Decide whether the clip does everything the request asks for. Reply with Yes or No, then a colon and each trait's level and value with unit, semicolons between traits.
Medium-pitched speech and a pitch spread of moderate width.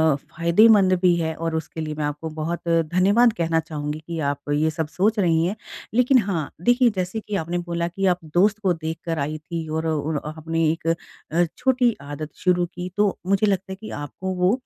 Yes: medium, 170 Hz; average, 3.4 semitones